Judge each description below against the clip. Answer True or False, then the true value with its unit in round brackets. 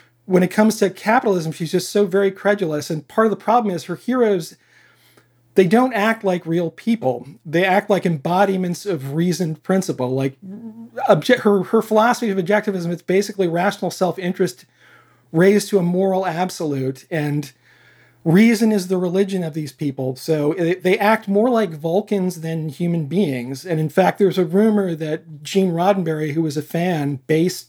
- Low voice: False (180 Hz)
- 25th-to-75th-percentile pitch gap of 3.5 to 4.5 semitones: True (4.1 semitones)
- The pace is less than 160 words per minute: False (170 wpm)